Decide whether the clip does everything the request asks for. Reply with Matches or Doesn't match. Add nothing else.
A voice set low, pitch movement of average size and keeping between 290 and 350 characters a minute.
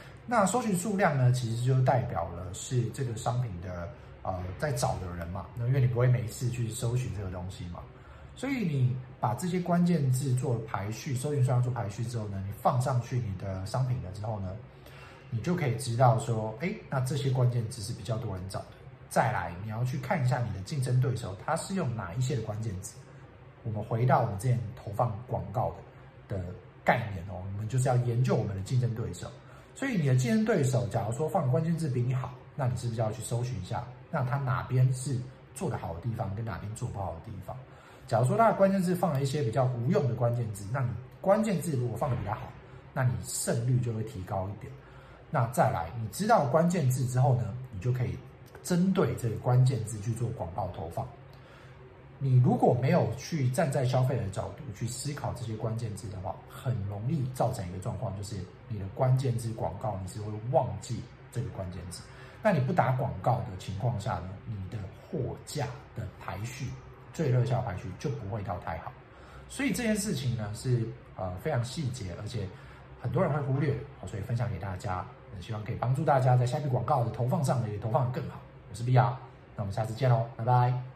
Matches